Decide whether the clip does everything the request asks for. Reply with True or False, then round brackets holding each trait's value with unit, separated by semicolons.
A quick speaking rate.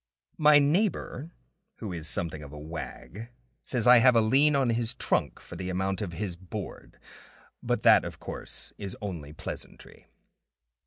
False (160 wpm)